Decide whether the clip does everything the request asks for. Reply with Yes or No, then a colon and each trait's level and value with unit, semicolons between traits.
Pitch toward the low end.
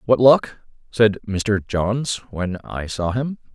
Yes: low, 110 Hz